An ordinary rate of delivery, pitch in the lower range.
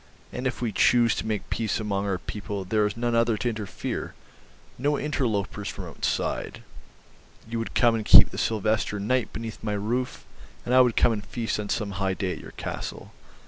Yes: average, 195 wpm; low, 110 Hz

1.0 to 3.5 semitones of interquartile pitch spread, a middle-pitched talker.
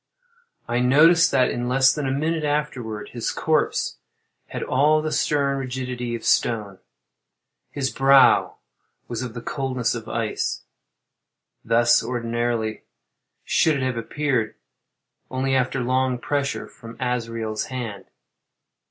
No: average, 2.8 semitones; low, 125 Hz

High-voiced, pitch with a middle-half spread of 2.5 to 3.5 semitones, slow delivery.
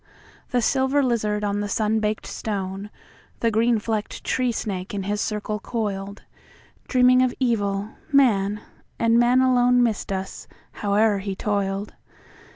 Yes: high, 215 Hz; average, 3.0 semitones; slow, 125 wpm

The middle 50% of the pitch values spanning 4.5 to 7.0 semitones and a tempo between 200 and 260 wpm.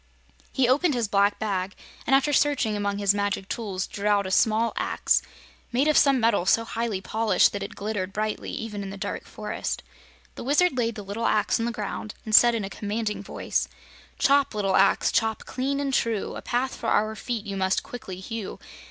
No: average, 3.0 semitones; fast, 205 wpm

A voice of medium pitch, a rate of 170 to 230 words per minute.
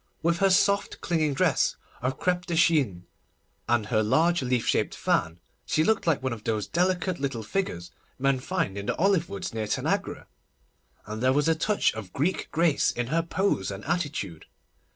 Yes: medium, 145 Hz; average, 180 wpm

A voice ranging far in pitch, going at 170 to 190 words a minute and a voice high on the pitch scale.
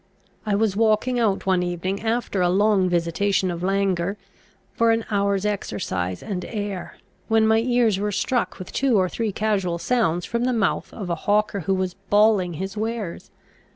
No: average, 3.2 semitones; average, 175 wpm; high, 200 Hz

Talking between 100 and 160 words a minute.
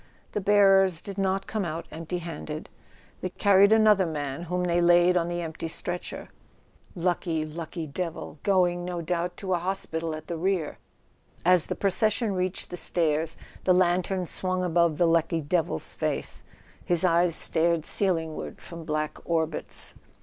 Yes: average, 155 wpm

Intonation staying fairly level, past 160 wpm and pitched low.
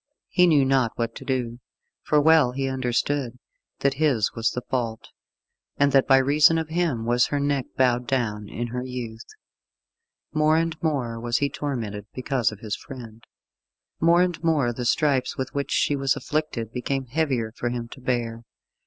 No: average, 3.4 semitones; average, 175 wpm; low, 130 Hz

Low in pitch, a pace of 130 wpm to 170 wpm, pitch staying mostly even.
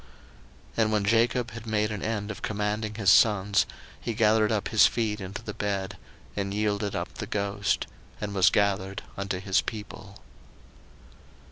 Yes: low, 105 Hz; average, 160 wpm; narrow, 1.5 semitones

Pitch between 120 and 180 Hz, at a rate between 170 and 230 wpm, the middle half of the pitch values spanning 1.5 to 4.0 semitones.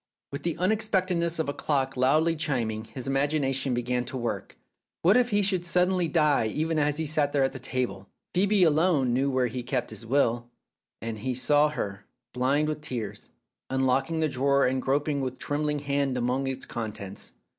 Yes: medium, 140 Hz; average, 190 wpm; average, 3.7 semitones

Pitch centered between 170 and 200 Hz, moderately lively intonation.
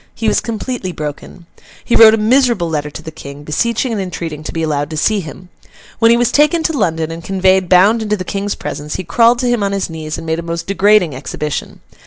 No: medium, 185 Hz; wide, 5.7 semitones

